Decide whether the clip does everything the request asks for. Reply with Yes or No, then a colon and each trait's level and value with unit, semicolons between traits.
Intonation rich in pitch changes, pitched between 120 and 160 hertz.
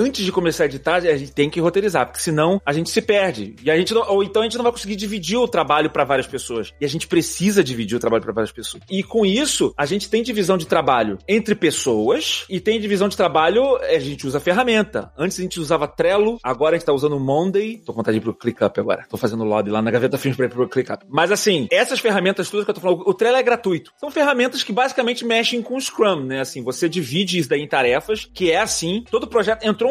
No: wide, 7.1 semitones; high, 190 Hz